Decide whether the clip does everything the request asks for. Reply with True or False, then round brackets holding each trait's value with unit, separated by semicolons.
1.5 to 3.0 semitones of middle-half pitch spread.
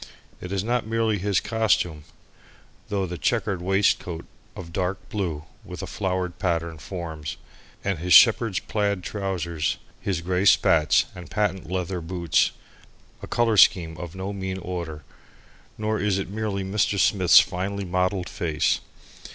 True (2.7 semitones)